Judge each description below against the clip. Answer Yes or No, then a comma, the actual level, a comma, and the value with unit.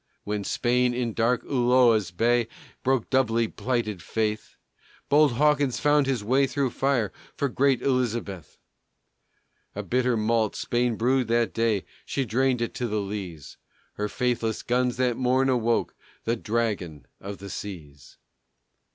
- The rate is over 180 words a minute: No, average, 140 wpm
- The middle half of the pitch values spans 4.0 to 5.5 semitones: No, average, 3.1 semitones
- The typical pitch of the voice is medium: No, low, 120 Hz